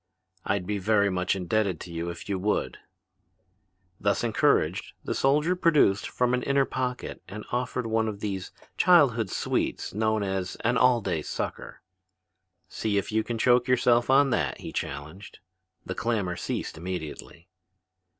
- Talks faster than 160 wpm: No, average, 150 wpm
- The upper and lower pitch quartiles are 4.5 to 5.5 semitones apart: Yes, average, 4.9 semitones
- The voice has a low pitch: Yes, low, 110 Hz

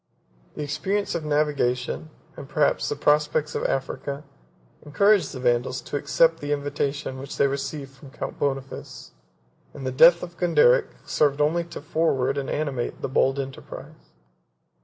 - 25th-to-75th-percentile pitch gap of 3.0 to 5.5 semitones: No, narrow, 2.4 semitones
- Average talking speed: Yes, average, 150 wpm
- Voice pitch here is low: No, medium, 145 Hz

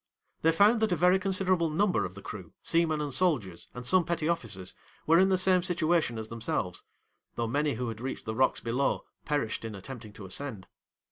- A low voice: No, medium, 145 Hz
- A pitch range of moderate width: No, wide, 7.8 semitones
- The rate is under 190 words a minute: No, average, 200 wpm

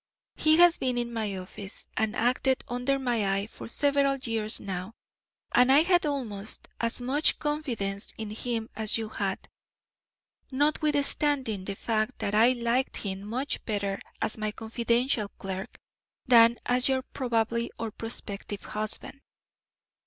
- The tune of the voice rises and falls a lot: No, average, 3.8 semitones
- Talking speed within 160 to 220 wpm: No, average, 140 wpm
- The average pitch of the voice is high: Yes, high, 230 Hz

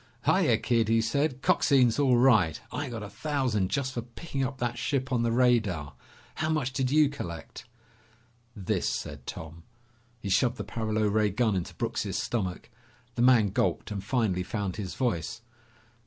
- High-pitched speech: No, low, 115 Hz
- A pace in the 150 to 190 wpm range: Yes, average, 170 wpm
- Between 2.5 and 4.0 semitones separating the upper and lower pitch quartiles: No, average, 4.4 semitones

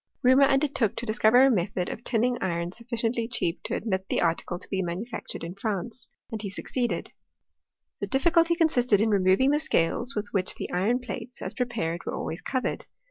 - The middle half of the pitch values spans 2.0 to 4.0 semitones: No, average, 5.0 semitones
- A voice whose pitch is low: No, high, 225 Hz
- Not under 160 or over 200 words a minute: Yes, average, 190 wpm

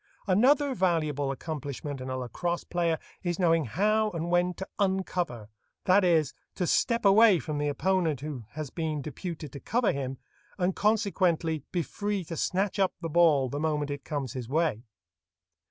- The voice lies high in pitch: No, medium, 165 Hz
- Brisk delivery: No, average, 165 wpm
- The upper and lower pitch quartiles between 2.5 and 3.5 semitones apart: No, average, 4.6 semitones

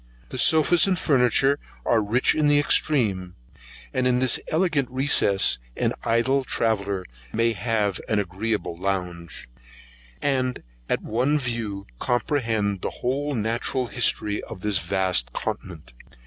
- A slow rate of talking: Yes, slow, 130 wpm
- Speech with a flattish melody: No, average, 5.0 semitones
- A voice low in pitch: Yes, low, 115 Hz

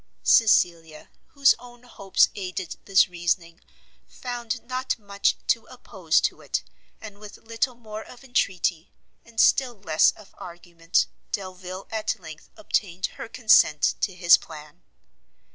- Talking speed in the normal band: No, slow, 130 wpm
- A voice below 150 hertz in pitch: No, high, 200 Hz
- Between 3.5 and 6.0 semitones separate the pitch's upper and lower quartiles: Yes, average, 5.0 semitones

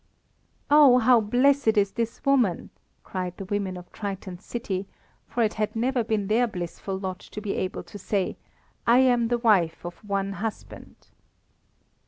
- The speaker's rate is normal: Yes, average, 160 wpm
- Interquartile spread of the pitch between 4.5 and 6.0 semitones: No, average, 3.8 semitones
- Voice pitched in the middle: No, high, 210 Hz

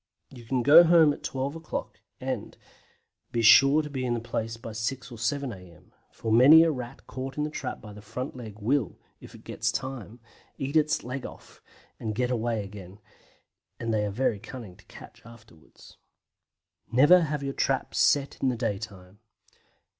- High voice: No, low, 120 Hz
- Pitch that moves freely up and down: No, average, 3.8 semitones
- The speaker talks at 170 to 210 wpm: Yes, average, 185 wpm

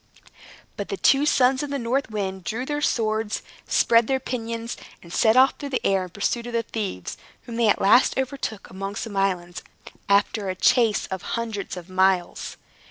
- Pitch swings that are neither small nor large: Yes, average, 4.3 semitones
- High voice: Yes, high, 220 Hz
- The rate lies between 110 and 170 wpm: No, average, 185 wpm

